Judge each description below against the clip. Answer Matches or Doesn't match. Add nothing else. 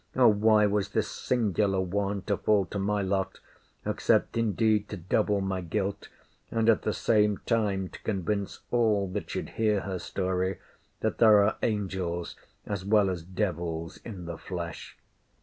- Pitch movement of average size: Doesn't match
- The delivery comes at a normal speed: Matches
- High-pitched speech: Doesn't match